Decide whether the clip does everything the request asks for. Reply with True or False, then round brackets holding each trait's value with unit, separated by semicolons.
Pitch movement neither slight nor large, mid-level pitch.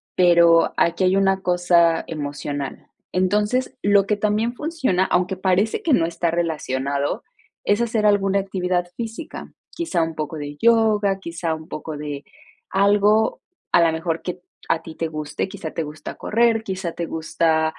True (4.1 semitones; 180 Hz)